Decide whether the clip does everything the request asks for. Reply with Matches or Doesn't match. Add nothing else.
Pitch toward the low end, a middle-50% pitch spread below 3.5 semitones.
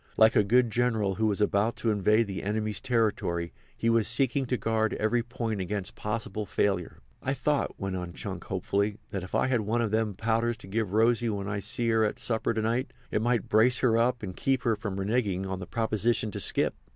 Matches